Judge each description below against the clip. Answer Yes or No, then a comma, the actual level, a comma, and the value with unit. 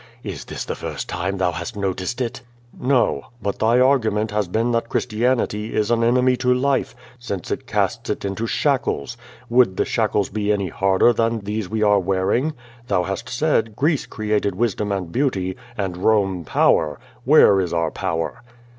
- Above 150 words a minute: Yes, average, 170 wpm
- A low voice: Yes, low, 105 Hz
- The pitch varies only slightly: No, average, 3.9 semitones